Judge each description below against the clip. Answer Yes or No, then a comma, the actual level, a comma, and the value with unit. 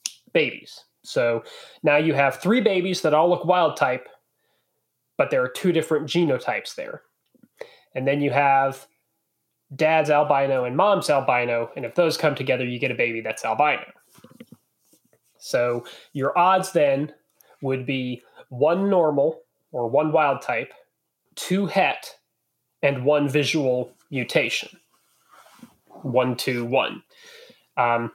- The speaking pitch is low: No, medium, 145 Hz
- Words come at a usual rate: No, slow, 130 wpm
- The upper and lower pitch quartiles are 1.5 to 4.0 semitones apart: No, wide, 5.6 semitones